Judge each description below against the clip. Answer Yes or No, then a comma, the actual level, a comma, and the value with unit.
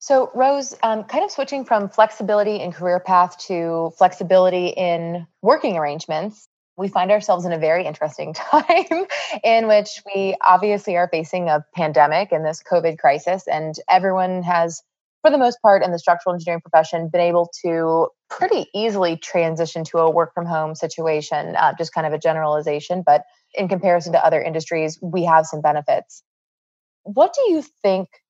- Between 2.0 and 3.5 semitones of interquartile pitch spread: No, average, 4.1 semitones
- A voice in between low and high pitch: Yes, medium, 180 Hz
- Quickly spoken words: No, average, 170 wpm